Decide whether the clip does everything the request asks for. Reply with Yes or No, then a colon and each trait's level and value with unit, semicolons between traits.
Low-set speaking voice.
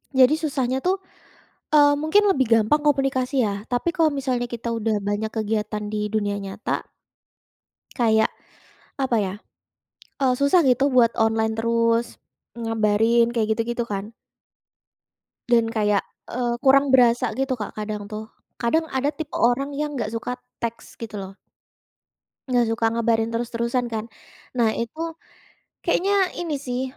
No: high, 235 Hz